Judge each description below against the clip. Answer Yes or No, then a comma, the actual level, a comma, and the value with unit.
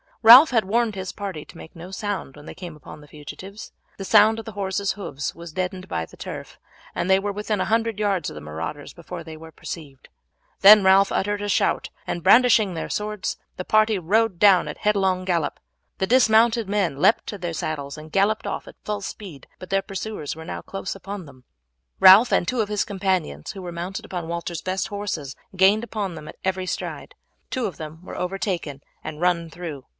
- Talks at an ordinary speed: No, fast, 210 wpm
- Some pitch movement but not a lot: Yes, average, 4.0 semitones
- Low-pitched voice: No, high, 190 Hz